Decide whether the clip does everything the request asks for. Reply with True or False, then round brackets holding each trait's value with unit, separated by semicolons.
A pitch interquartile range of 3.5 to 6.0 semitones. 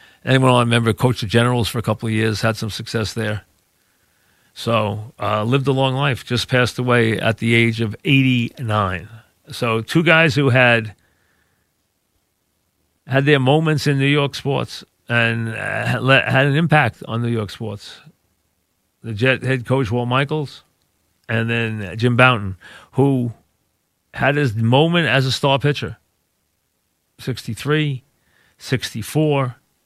True (3.9 semitones)